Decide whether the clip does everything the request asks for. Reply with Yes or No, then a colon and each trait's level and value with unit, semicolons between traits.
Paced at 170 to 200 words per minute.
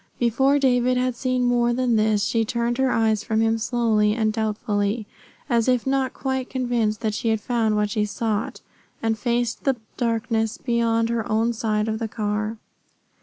Yes: average, 175 wpm